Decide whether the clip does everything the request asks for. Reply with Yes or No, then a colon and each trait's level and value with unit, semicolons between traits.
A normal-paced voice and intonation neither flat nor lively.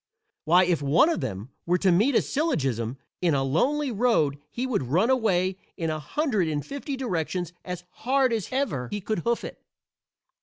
No: average, 185 wpm; wide, 8.4 semitones